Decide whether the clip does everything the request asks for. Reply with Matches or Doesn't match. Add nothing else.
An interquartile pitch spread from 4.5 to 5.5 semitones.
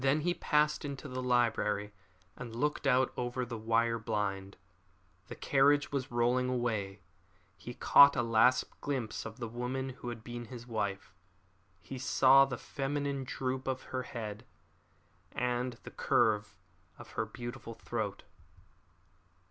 Doesn't match